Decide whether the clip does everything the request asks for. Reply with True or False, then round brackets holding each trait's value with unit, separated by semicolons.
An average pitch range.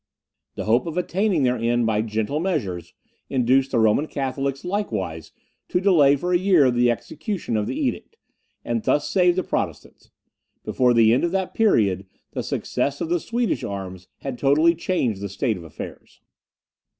False (8.0 semitones)